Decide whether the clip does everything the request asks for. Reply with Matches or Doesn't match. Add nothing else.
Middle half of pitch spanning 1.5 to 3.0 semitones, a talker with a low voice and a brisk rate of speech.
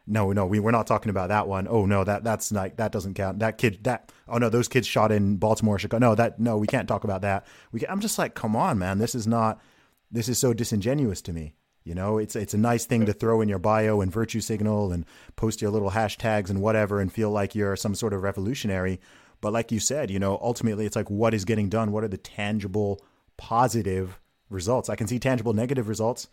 Matches